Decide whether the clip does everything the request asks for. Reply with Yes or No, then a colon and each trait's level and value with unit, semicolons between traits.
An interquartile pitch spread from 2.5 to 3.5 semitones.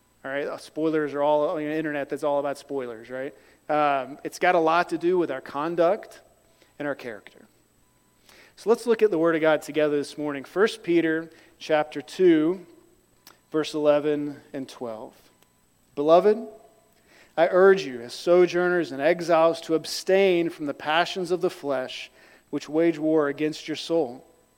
Yes: average, 3.1 semitones